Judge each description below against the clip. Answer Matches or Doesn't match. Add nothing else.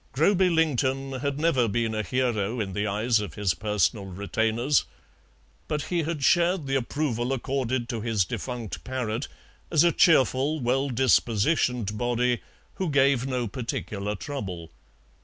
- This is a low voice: Matches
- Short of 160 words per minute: Matches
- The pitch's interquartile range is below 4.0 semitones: Doesn't match